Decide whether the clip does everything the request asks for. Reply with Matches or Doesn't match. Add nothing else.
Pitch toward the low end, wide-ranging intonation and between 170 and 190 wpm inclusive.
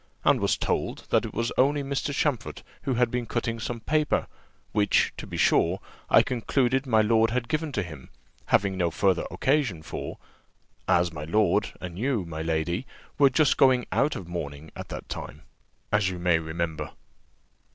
Matches